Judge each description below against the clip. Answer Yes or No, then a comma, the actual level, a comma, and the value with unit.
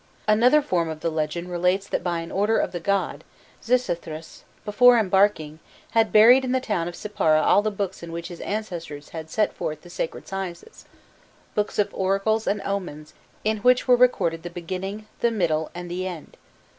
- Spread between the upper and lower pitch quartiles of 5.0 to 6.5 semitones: No, average, 4.2 semitones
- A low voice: No, high, 190 Hz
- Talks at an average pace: Yes, average, 190 wpm